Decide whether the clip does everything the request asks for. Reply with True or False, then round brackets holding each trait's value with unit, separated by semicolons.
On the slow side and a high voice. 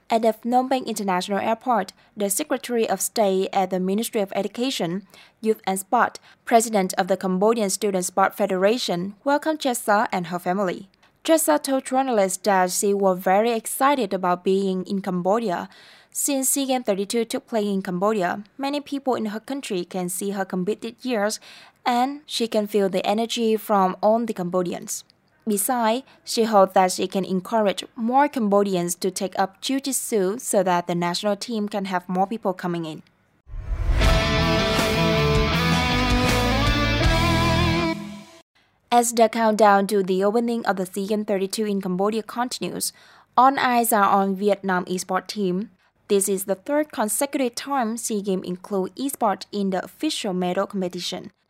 True (150 wpm; 200 Hz)